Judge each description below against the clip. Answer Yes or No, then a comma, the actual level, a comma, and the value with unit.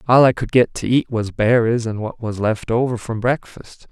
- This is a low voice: Yes, low, 115 Hz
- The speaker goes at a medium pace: No, fast, 230 wpm